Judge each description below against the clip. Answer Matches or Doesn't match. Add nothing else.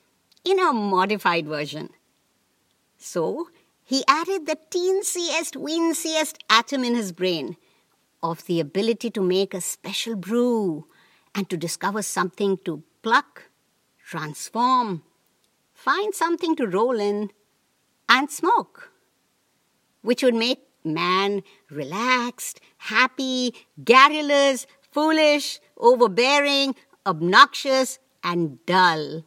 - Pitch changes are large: Matches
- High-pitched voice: Matches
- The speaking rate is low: Matches